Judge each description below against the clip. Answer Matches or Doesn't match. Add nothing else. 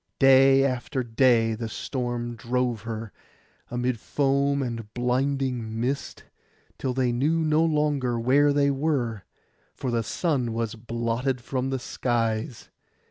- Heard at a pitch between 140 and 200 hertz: Doesn't match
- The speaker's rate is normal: Doesn't match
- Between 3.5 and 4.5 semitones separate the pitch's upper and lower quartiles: Doesn't match